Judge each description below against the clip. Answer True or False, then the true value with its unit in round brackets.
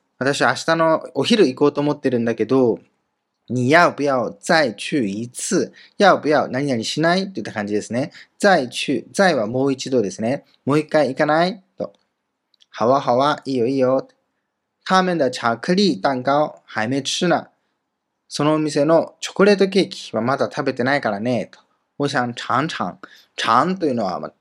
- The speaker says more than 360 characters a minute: False (350 characters per minute)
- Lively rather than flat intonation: False (4.4 semitones)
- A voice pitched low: False (145 Hz)